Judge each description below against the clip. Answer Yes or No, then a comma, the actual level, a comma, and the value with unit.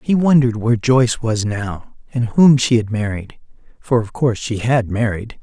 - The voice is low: Yes, low, 115 Hz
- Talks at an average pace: Yes, average, 190 wpm